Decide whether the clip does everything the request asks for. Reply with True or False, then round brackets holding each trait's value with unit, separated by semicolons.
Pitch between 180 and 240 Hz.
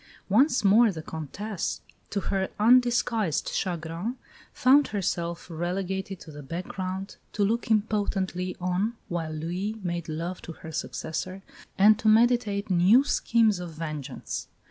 True (190 Hz)